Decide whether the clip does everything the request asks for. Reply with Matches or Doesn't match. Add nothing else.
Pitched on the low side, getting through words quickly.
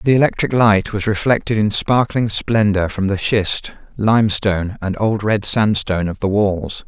Doesn't match